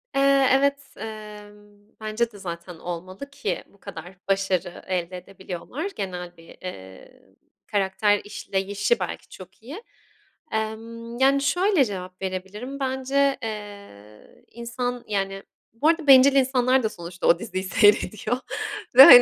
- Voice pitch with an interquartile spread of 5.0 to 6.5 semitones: Yes, wide, 5.5 semitones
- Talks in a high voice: Yes, high, 210 Hz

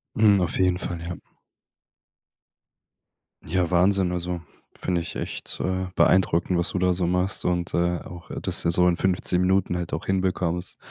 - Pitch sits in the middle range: No, very low, 90 Hz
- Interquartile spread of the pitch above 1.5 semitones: No, narrow, 1.2 semitones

